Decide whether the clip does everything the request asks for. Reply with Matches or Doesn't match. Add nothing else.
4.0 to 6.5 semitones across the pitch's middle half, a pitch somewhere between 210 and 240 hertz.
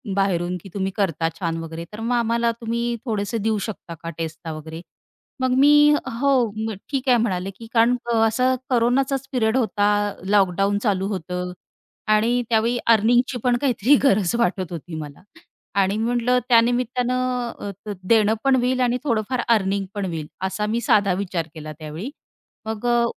Matches